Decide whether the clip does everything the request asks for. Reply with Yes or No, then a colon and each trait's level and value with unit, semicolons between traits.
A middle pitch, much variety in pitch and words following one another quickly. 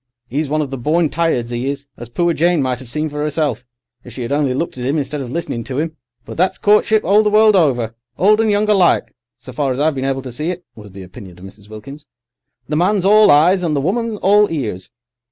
Yes: medium, 150 Hz; wide, 5.9 semitones; fast, 245 wpm